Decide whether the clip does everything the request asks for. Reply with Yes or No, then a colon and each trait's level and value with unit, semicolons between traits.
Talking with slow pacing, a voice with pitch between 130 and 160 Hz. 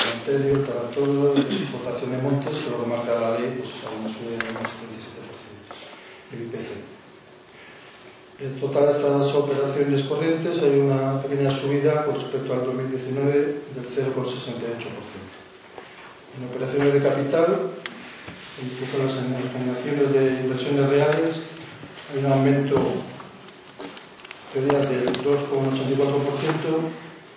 Yes: slow, 110 wpm; medium, 140 Hz